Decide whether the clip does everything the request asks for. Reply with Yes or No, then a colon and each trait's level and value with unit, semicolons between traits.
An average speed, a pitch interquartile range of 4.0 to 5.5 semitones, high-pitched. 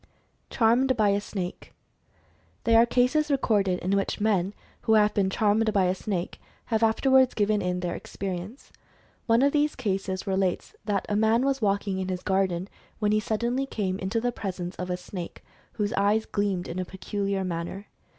No: average, 180 wpm; average, 3.2 semitones; high, 205 Hz